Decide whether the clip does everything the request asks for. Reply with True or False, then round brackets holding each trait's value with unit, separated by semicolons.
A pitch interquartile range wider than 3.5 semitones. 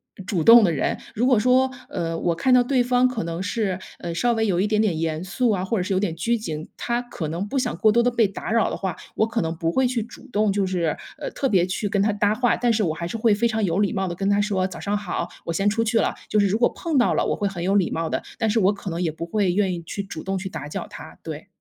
True (4.5 semitones)